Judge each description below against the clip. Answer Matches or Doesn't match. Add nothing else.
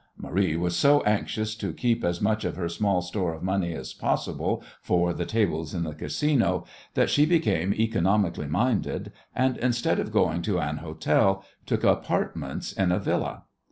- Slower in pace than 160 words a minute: Doesn't match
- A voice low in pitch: Matches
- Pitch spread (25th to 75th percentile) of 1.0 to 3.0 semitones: Doesn't match